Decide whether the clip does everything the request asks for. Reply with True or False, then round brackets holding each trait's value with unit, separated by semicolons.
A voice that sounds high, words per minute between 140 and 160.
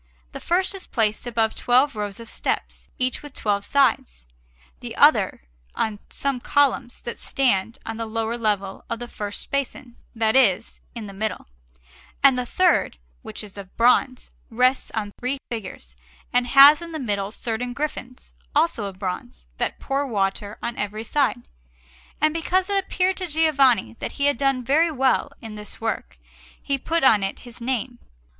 False (240 Hz; 170 wpm)